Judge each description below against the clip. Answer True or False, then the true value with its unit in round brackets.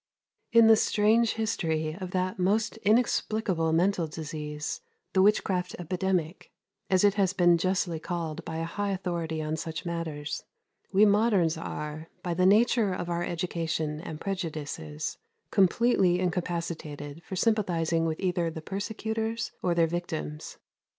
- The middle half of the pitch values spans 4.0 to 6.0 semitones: False (3.6 semitones)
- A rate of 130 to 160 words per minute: True (140 wpm)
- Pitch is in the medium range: True (175 Hz)